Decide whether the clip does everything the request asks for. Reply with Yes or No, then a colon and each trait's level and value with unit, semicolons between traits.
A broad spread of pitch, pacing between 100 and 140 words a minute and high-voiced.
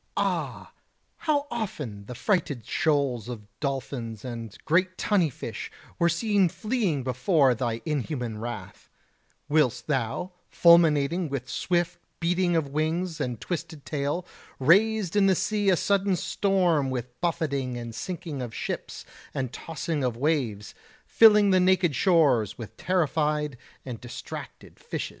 No: wide, 6.3 semitones; slow, 135 wpm; medium, 155 Hz